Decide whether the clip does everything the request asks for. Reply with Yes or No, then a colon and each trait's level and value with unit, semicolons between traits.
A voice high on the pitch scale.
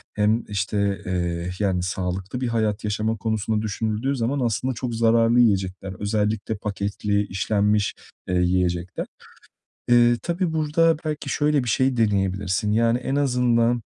No: low, 110 Hz